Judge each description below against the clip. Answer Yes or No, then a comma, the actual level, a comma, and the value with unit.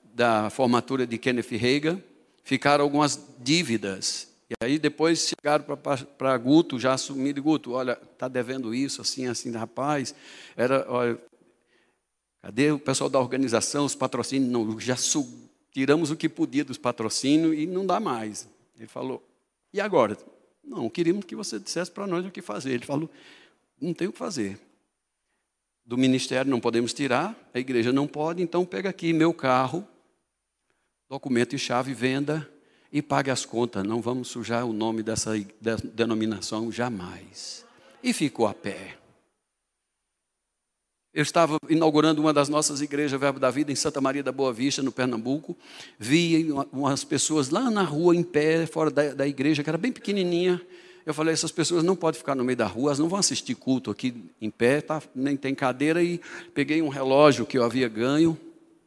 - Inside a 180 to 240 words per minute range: No, average, 165 wpm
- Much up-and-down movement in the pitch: No, average, 4.3 semitones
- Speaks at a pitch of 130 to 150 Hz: Yes, medium, 140 Hz